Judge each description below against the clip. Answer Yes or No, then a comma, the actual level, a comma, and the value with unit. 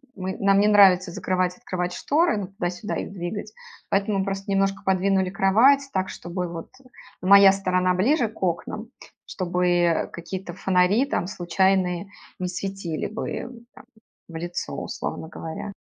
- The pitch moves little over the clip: Yes, narrow, 1.8 semitones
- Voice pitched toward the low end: No, high, 190 Hz